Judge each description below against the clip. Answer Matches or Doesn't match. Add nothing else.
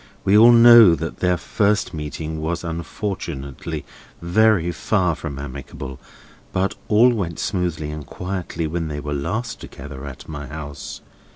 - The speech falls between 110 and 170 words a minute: Matches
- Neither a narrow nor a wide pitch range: Matches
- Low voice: Matches